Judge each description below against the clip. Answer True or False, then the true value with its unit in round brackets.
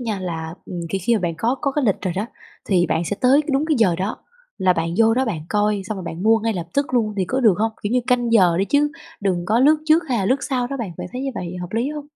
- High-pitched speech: True (215 Hz)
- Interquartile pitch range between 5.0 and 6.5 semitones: True (5.5 semitones)